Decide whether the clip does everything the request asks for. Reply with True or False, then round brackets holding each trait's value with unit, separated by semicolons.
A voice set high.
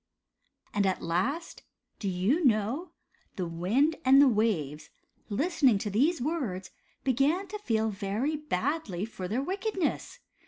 True (235 Hz)